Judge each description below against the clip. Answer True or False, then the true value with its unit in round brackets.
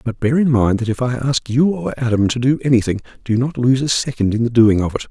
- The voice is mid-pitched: False (125 Hz)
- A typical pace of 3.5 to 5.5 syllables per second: False (5.9 syllables/s)